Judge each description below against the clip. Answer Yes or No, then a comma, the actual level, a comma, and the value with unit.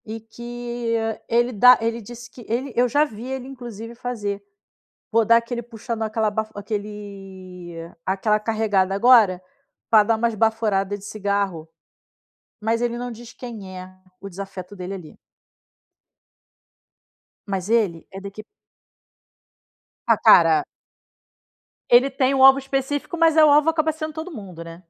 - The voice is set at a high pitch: Yes, high, 225 Hz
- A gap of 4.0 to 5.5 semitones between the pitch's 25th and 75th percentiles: No, average, 3.5 semitones